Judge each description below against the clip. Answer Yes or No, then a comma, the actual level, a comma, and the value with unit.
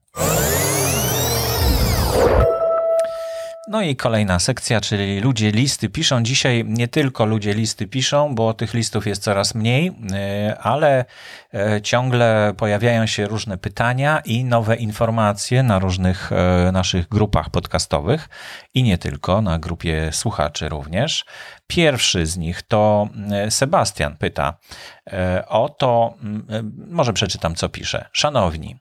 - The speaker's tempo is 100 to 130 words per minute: Yes, slow, 110 wpm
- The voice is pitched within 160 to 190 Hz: No, low, 110 Hz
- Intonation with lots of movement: No, average, 4.3 semitones